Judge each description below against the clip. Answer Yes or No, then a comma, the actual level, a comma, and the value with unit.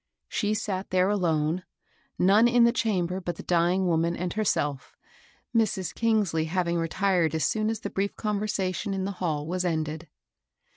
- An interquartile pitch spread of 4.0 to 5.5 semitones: No, average, 3.6 semitones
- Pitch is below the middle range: No, medium, 185 Hz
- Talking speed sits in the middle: Yes, average, 160 wpm